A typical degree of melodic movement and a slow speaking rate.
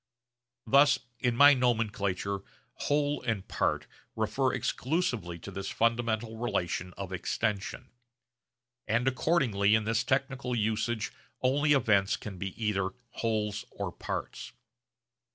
Yes: average, 4.2 semitones; slow, 115 wpm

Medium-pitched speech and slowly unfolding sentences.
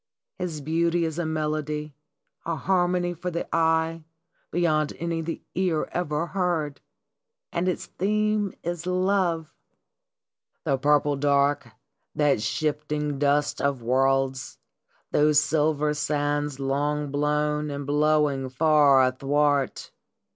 Yes: medium, 150 Hz; slow, 115 wpm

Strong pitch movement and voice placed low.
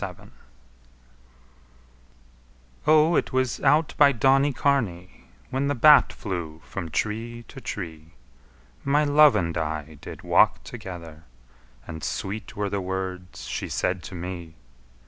Yes: wide, 8.1 semitones; low, 100 Hz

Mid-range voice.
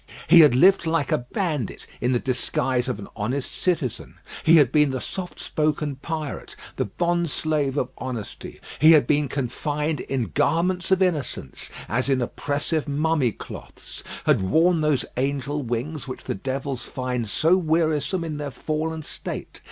Yes: medium, 145 Hz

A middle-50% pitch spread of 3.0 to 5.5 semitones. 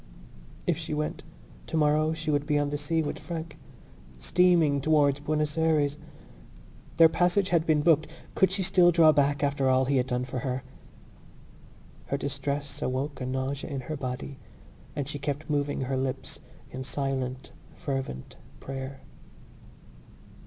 No: narrow, 2.6 semitones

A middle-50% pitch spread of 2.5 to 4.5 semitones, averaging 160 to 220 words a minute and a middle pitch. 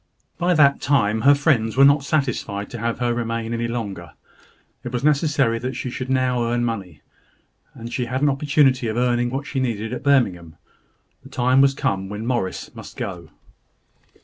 No: average, 3.4 semitones; average, 180 wpm; low, 120 Hz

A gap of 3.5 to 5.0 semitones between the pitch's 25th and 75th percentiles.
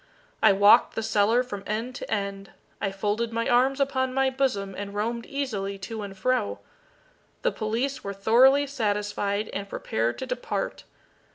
Yes: average, 4.2 semitones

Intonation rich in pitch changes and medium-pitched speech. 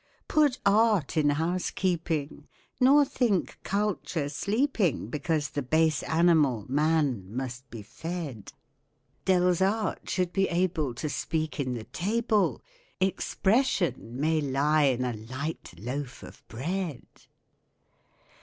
Yes: wide, 5.7 semitones; medium, 160 Hz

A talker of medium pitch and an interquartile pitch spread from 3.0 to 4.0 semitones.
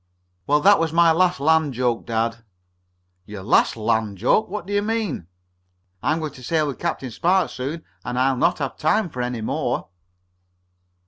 No: medium, 145 Hz; wide, 5.6 semitones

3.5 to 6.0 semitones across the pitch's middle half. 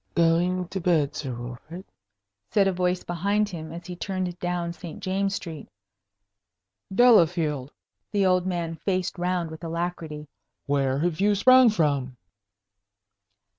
No: average, 2.9 semitones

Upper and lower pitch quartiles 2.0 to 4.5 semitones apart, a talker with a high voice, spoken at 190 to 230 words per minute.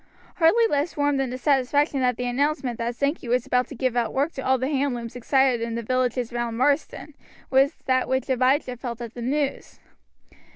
Yes: narrow, 2.6 semitones; very high, 260 Hz; fast, 205 wpm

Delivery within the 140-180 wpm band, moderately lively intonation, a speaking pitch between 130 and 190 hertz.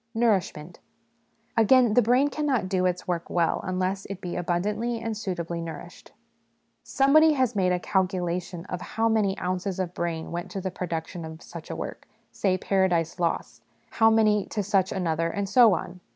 Yes: average, 170 wpm; average, 3.9 semitones; medium, 185 Hz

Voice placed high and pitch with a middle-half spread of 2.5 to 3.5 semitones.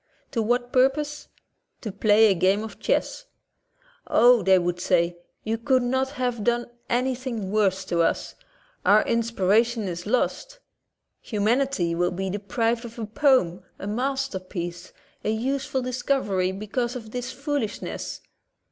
No: high, 225 Hz; average, 4.8 semitones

